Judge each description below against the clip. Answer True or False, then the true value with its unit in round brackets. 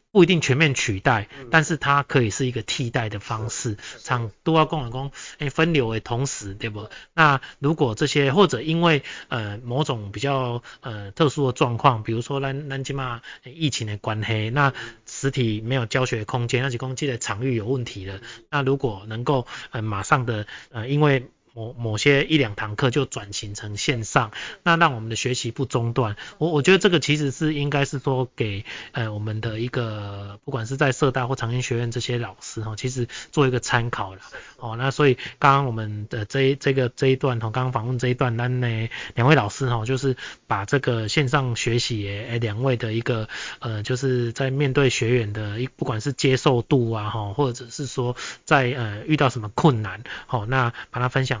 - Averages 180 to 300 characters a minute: True (290 characters per minute)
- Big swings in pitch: False (3.5 semitones)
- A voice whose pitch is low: True (125 Hz)